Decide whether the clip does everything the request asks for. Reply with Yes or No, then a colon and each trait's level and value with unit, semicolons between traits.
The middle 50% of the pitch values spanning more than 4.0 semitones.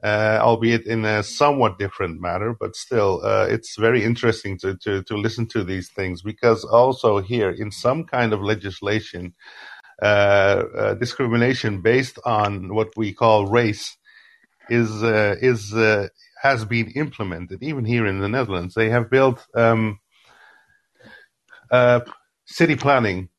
No: average, 3.0 semitones